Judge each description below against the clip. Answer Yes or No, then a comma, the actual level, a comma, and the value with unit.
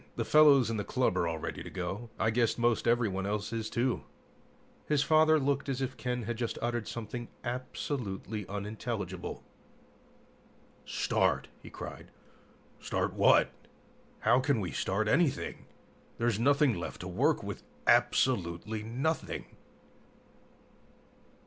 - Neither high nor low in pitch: No, low, 115 Hz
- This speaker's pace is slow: Yes, slow, 130 wpm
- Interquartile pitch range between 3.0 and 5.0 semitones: Yes, average, 3.9 semitones